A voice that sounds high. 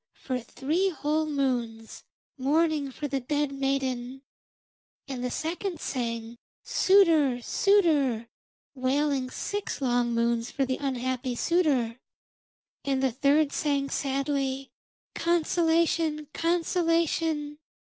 Yes: very high, 275 Hz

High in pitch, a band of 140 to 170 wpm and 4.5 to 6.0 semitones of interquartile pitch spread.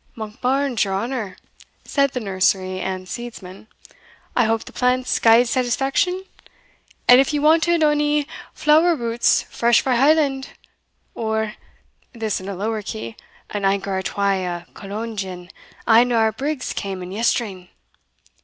Yes: high, 225 Hz; average, 145 wpm; wide, 5.4 semitones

